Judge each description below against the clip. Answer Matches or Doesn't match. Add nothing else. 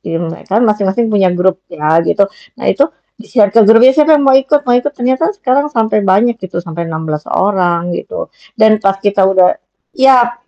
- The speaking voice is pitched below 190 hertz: Doesn't match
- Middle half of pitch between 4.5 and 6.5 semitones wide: Matches